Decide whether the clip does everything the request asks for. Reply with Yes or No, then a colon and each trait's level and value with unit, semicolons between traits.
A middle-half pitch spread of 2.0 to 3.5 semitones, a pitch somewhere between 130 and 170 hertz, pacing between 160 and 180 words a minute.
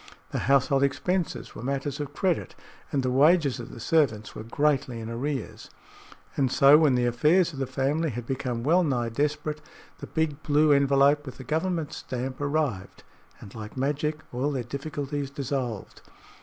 Yes: average, 3.0 semitones; medium, 140 Hz; average, 170 wpm